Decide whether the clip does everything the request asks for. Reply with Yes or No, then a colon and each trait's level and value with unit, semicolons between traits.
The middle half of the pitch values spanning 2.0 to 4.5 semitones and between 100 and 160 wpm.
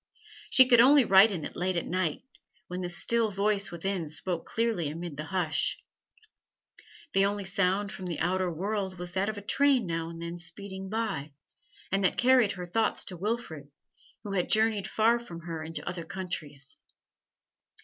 No: average, 3.7 semitones; average, 175 wpm